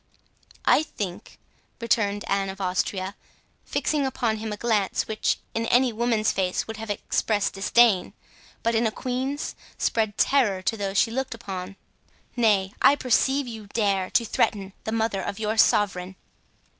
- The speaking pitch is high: Yes, high, 215 Hz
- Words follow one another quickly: No, average, 155 wpm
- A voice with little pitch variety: No, average, 3.0 semitones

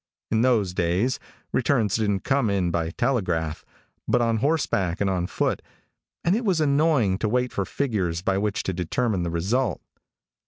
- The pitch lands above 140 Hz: No, low, 105 Hz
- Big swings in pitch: Yes, wide, 5.9 semitones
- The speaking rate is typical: Yes, average, 165 wpm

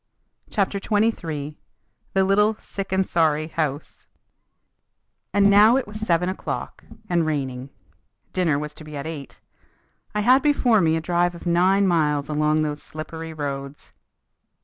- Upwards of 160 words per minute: No, average, 145 wpm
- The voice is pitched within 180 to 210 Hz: No, medium, 165 Hz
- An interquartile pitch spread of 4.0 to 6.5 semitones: Yes, average, 4.7 semitones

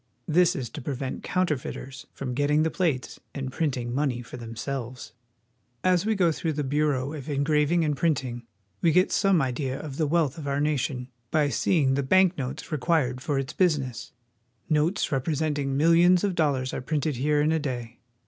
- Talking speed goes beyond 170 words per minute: Yes, average, 185 wpm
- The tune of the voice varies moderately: Yes, average, 3.6 semitones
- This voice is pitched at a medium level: Yes, medium, 145 Hz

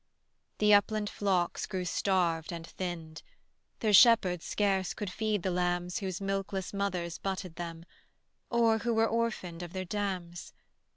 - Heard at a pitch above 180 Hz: Yes, high, 190 Hz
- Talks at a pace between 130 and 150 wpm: Yes, average, 140 wpm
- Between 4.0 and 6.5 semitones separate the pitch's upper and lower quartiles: No, average, 2.8 semitones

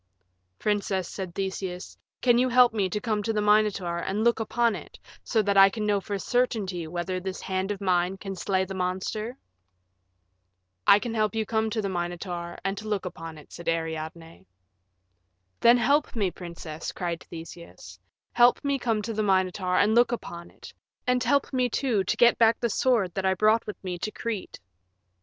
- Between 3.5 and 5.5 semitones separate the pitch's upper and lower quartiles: Yes, average, 3.8 semitones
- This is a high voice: Yes, high, 200 Hz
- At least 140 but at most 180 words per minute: No, average, 190 wpm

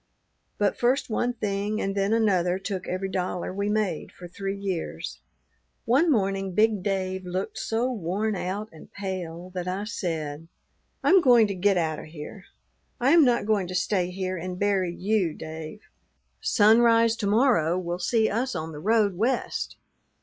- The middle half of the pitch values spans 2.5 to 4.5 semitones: Yes, average, 3.3 semitones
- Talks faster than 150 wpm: Yes, average, 170 wpm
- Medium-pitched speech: No, high, 195 Hz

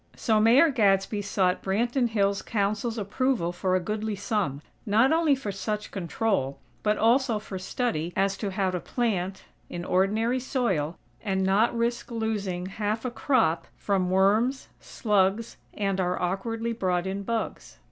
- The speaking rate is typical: Yes, average, 150 wpm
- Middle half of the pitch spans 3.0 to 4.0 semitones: Yes, average, 3.3 semitones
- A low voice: No, high, 205 Hz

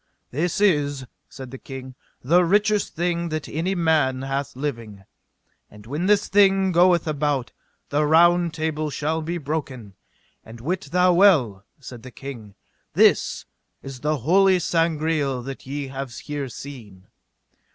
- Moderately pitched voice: Yes, medium, 150 Hz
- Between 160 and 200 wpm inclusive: No, average, 140 wpm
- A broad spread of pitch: No, average, 4.6 semitones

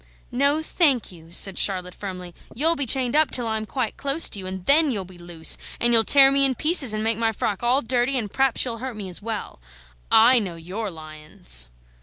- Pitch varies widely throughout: Yes, wide, 6.2 semitones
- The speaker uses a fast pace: Yes, fast, 220 wpm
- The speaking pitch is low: No, high, 225 Hz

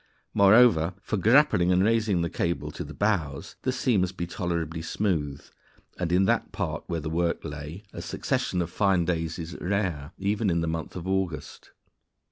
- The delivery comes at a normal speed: Yes, average, 180 wpm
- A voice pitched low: Yes, very low, 90 Hz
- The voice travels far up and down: No, average, 3.3 semitones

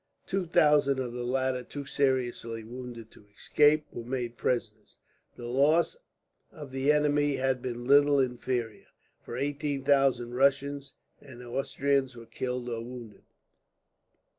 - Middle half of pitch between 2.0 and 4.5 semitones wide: Yes, average, 2.7 semitones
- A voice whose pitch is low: Yes, low, 130 Hz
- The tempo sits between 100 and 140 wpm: Yes, slow, 135 wpm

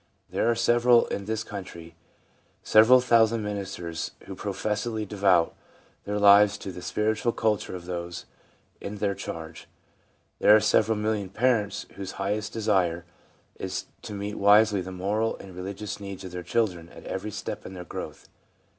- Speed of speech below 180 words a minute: Yes, average, 155 wpm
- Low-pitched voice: Yes, low, 100 Hz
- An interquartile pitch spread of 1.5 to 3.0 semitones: Yes, average, 2.7 semitones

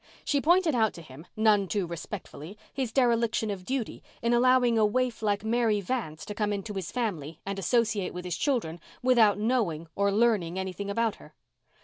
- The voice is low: No, high, 210 Hz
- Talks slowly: No, average, 185 wpm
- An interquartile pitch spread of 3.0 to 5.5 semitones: Yes, average, 3.9 semitones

